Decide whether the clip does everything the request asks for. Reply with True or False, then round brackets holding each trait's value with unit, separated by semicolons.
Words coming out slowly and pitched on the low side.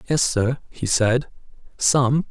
True (130 wpm; 130 Hz)